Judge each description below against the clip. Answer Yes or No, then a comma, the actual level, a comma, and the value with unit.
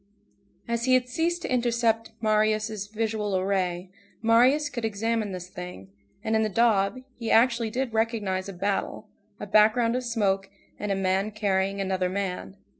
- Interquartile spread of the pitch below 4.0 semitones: Yes, average, 3.1 semitones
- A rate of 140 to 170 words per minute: Yes, average, 160 wpm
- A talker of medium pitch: No, high, 215 Hz